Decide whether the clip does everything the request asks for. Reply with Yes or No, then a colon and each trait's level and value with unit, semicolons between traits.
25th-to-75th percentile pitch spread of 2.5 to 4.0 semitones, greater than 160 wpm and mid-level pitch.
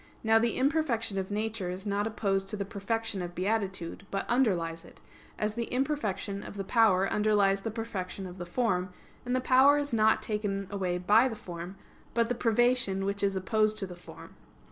No: average, 3.0 semitones; average, 190 wpm; high, 205 Hz